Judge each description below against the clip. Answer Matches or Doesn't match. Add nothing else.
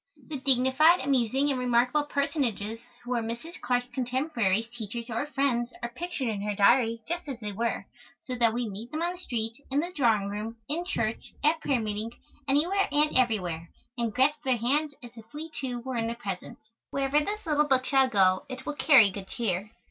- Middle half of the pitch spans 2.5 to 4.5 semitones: Matches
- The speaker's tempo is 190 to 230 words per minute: Matches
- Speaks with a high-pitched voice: Matches